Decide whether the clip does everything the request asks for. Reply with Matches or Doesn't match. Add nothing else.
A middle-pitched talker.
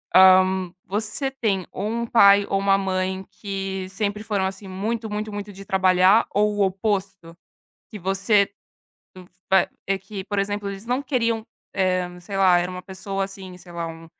Doesn't match